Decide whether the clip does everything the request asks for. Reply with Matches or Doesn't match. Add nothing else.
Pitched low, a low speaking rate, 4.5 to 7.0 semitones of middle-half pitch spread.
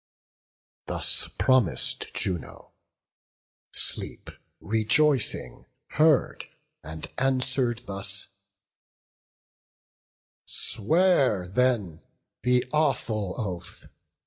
Matches